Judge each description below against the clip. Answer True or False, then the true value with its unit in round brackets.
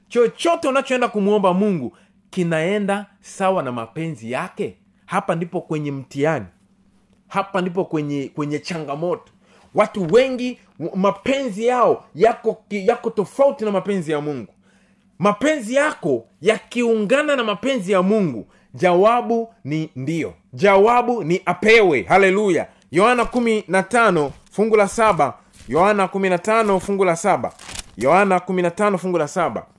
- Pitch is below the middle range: False (200 Hz)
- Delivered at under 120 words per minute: True (110 wpm)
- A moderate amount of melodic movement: True (4.7 semitones)